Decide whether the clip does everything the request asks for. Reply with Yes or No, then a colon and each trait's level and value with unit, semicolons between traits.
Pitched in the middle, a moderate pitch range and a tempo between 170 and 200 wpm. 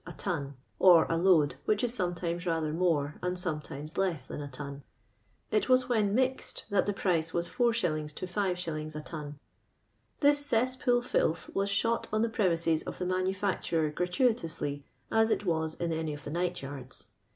Yes: medium, 175 Hz; average, 4.8 semitones; average, 180 wpm